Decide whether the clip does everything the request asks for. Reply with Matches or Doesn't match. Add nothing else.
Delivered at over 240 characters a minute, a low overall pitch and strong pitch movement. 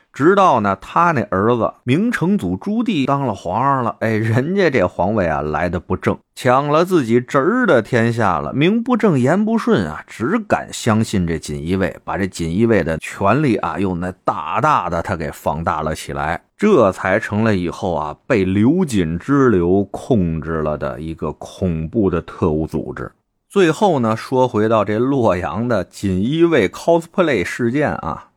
Matches